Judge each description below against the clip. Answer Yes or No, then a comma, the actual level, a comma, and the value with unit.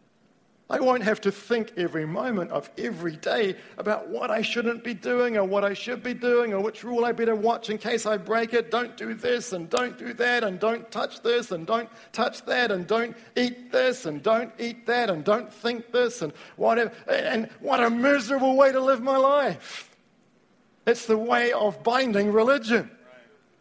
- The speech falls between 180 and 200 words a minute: Yes, average, 195 wpm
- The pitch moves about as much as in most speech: No, narrow, 2.1 semitones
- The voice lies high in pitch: Yes, high, 230 Hz